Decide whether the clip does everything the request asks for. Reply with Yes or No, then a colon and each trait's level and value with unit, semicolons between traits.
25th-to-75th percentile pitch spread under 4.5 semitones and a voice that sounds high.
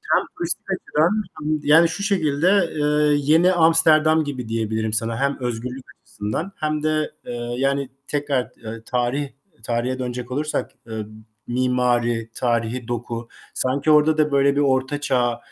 No: average, 4.1 semitones; low, 135 Hz